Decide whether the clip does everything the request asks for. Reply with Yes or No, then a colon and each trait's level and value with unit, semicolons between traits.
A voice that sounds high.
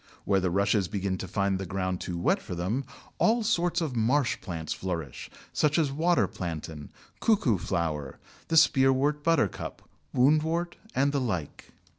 No: low, 110 Hz